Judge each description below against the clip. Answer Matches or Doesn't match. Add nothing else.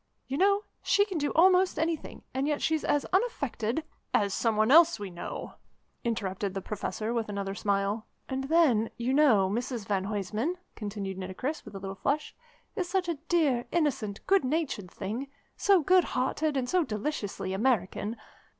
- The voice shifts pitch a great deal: Matches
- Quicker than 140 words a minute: Matches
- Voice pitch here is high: Matches